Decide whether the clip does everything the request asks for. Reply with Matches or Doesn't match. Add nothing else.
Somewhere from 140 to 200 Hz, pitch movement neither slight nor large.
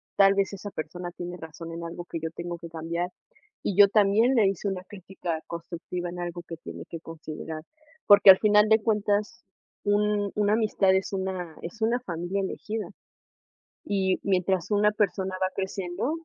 Matches